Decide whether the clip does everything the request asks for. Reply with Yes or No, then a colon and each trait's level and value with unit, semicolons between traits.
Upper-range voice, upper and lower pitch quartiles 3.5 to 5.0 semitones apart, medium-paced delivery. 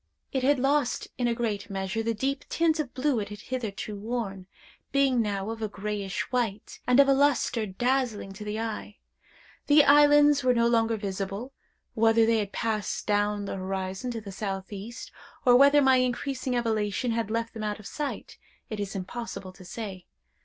Yes: high, 225 Hz; average, 3.8 semitones; average, 180 wpm